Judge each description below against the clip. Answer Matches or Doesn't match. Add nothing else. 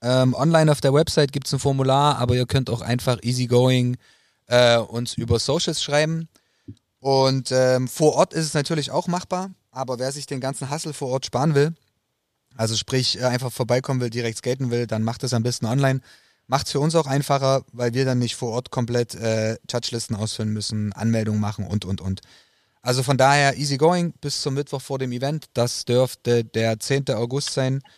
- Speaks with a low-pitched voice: Matches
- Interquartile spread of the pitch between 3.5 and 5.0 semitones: Doesn't match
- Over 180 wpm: Matches